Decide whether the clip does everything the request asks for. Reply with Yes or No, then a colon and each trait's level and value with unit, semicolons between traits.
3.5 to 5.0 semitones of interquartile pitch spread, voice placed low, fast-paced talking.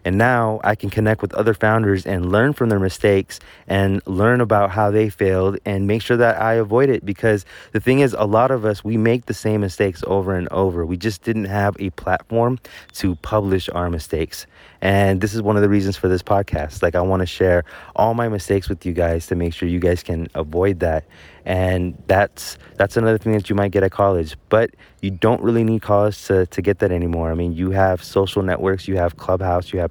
No: average, 3.0 semitones; low, 100 Hz; fast, 230 wpm